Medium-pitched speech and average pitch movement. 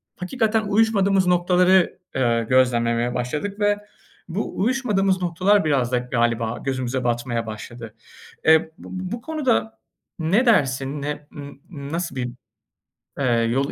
No: medium, 145 Hz; wide, 8.0 semitones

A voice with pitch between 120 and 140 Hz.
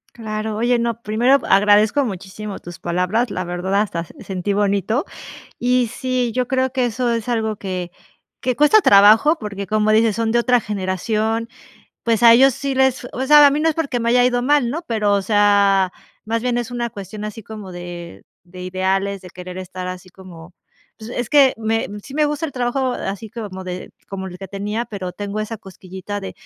No: high, 215 Hz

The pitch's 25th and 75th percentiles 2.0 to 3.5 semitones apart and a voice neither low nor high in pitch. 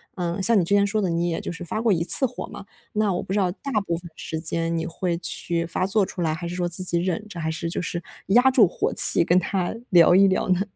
Yes: average, 2.8 semitones; medium, 180 Hz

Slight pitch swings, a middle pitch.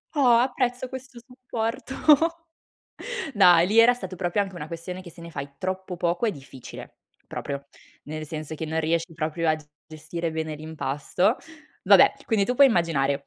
No: wide, 6.6 semitones; medium, 175 Hz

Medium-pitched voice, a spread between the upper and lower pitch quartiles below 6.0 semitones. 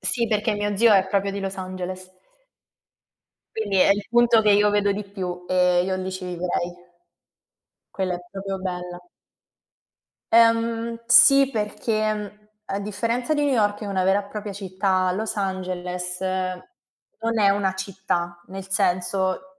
No: high, 195 Hz; narrow, 2.4 semitones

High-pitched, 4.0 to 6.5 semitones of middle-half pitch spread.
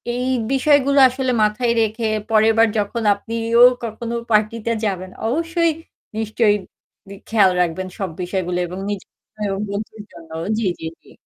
No: high, 220 Hz; average, 2.8 semitones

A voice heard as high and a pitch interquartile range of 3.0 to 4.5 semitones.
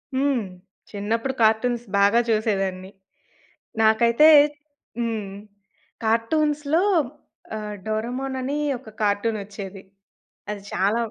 Yes: high, 220 Hz; average, 3.3 semitones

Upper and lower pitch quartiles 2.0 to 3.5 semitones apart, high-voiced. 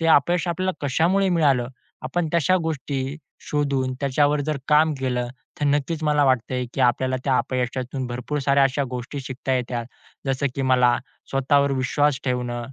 No: narrow, 2.6 semitones; low, 135 Hz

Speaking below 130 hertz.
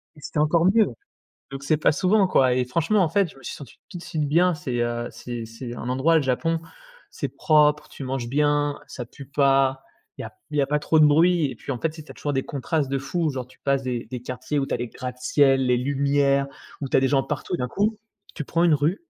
No: medium, 140 Hz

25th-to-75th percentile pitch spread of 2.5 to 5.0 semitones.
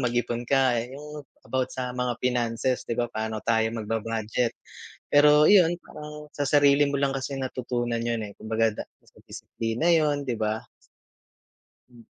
Yes: average, 3.8 semitones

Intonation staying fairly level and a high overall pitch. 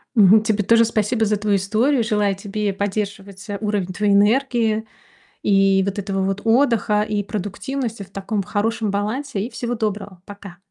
Yes: narrow, 2.0 semitones; high, 210 Hz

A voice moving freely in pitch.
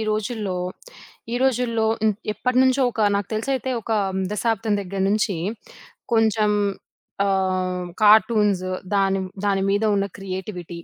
No: narrow, 2.5 semitones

